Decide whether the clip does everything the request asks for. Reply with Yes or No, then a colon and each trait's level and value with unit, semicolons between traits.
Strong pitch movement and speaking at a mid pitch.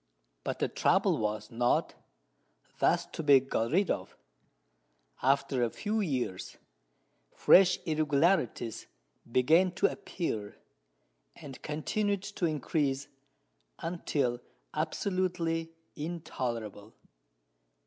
Yes: wide, 6.1 semitones; medium, 150 Hz